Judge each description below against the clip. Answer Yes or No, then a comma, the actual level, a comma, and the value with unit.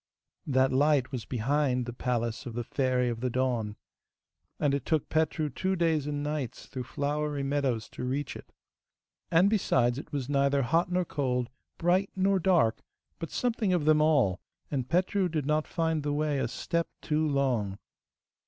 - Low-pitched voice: No, medium, 145 Hz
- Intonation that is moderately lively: Yes, average, 4.0 semitones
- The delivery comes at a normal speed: Yes, average, 170 wpm